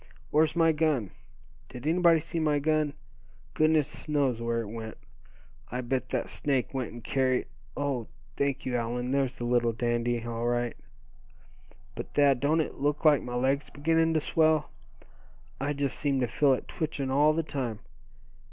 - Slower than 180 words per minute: Yes, average, 165 wpm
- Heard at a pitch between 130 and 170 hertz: Yes, medium, 140 Hz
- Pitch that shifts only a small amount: No, average, 3.9 semitones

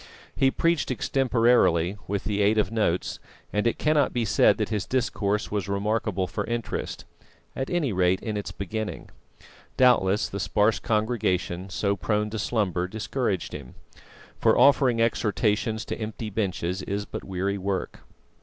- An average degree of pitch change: Yes, average, 3.0 semitones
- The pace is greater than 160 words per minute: No, average, 150 wpm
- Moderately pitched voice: No, low, 105 Hz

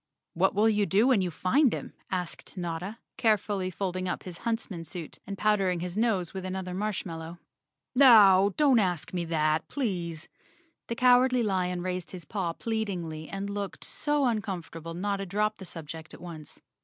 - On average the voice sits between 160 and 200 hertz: Yes, high, 190 Hz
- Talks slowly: No, average, 165 wpm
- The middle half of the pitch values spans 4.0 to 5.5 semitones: No, average, 3.5 semitones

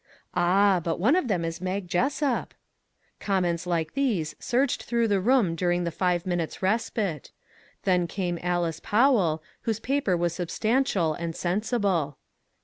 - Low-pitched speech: No, medium, 185 Hz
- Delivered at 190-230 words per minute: No, average, 155 wpm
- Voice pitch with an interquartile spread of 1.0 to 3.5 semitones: No, average, 4.7 semitones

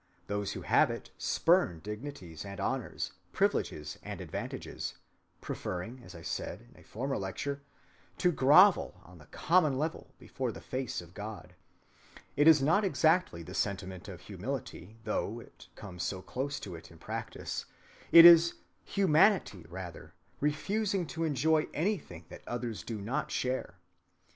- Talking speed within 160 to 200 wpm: No, average, 150 wpm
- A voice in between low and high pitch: No, low, 125 Hz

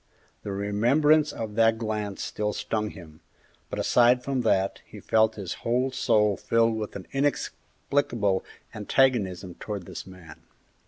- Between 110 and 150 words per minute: Yes, average, 140 wpm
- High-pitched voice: No, low, 110 Hz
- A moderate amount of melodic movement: Yes, average, 3.5 semitones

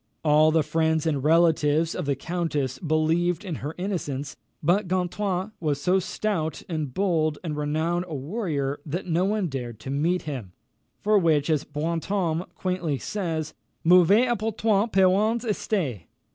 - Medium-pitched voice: Yes, medium, 165 Hz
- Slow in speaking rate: No, average, 150 wpm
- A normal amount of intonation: Yes, average, 3.8 semitones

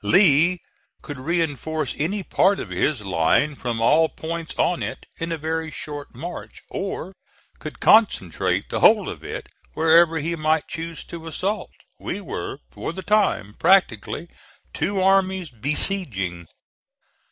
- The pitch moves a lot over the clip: No, average, 4.0 semitones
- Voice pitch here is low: No, medium, 160 Hz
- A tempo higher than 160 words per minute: No, average, 140 wpm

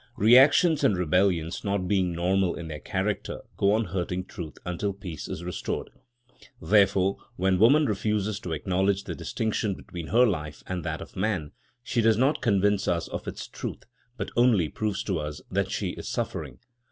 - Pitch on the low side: Yes, very low, 95 Hz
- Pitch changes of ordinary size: Yes, average, 3.5 semitones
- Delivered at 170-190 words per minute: Yes, average, 175 wpm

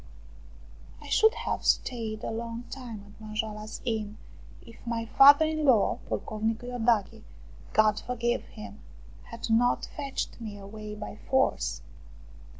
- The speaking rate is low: Yes, slow, 130 wpm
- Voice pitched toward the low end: No, high, 225 Hz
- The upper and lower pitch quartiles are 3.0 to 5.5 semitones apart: No, narrow, 2.5 semitones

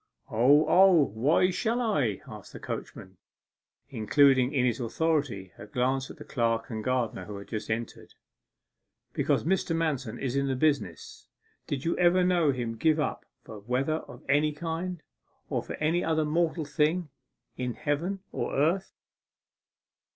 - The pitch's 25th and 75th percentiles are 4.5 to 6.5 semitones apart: Yes, average, 5.3 semitones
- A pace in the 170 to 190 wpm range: No, average, 160 wpm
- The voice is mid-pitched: Yes, medium, 145 Hz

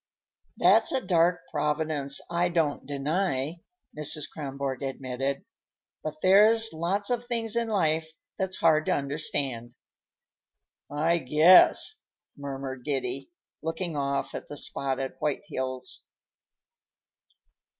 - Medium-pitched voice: Yes, medium, 150 Hz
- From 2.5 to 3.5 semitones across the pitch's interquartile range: No, average, 4.2 semitones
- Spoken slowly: Yes, slow, 110 wpm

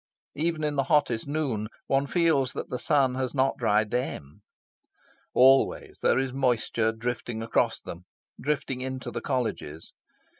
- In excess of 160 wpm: No, average, 140 wpm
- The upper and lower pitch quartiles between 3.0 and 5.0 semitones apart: Yes, average, 3.5 semitones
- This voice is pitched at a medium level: No, low, 130 Hz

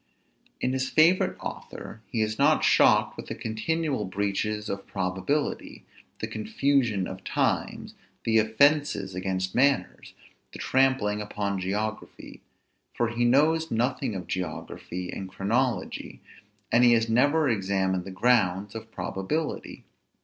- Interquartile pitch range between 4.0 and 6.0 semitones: Yes, average, 5.2 semitones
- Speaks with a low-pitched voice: Yes, low, 110 Hz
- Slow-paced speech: Yes, slow, 130 wpm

